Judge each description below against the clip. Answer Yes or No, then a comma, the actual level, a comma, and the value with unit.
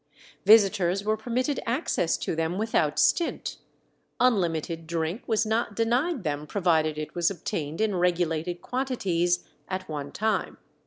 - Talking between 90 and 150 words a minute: Yes, slow, 135 wpm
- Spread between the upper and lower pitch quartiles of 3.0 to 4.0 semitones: No, average, 5.3 semitones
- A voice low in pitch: No, medium, 180 Hz